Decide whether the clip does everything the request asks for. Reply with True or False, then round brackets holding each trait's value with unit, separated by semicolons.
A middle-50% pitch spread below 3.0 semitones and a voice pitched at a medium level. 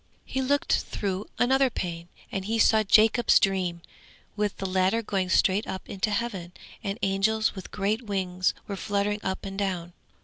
False (2.5 semitones; 195 Hz)